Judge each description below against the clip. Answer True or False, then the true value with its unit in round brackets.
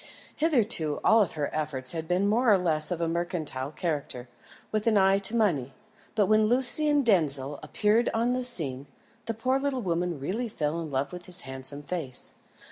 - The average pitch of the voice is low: False (180 Hz)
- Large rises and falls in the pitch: True (7.2 semitones)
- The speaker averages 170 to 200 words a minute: True (180 wpm)